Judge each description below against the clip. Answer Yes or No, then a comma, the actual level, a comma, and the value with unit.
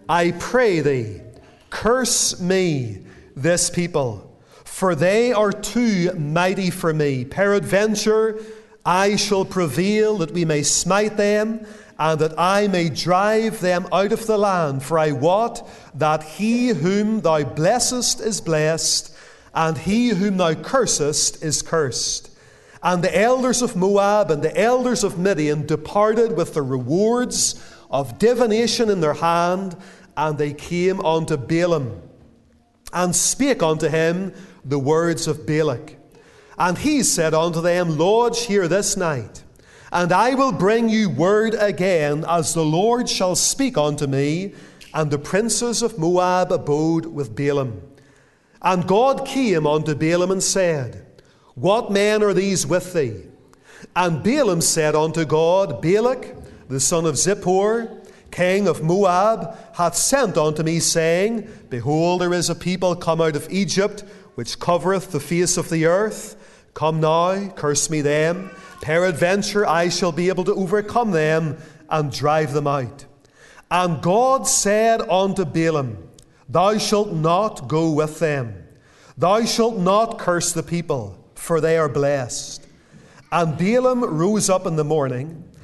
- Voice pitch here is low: No, medium, 175 Hz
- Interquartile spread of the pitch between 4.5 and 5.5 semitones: Yes, average, 4.8 semitones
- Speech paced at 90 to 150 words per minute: Yes, average, 145 wpm